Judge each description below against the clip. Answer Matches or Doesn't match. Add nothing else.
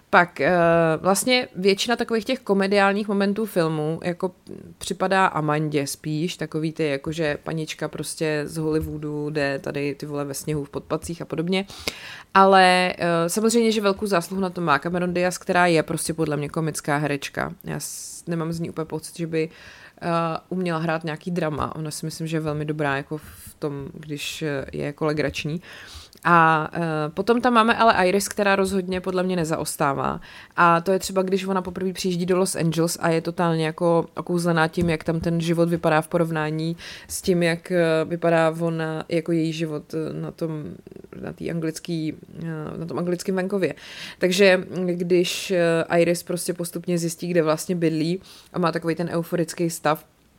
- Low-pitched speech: Doesn't match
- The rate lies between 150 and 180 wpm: Matches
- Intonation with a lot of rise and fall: Doesn't match